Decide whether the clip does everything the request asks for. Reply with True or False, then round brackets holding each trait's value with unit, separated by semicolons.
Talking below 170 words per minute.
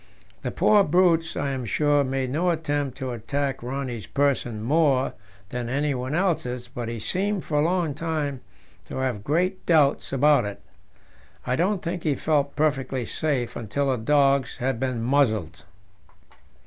True (155 wpm)